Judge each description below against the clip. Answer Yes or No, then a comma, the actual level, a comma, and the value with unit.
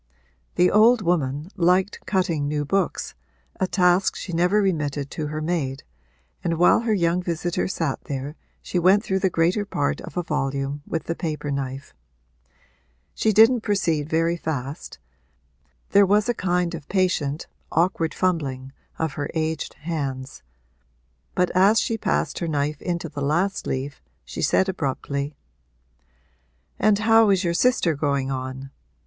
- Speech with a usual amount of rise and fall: Yes, average, 4.6 semitones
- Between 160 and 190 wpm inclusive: No, average, 150 wpm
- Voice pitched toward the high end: No, medium, 165 Hz